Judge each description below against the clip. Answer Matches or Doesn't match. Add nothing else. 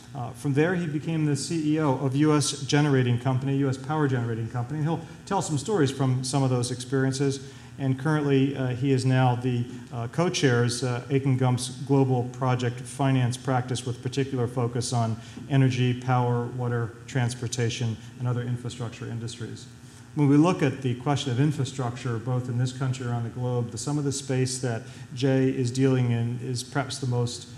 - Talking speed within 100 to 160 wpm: Doesn't match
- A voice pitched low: Matches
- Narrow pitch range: Matches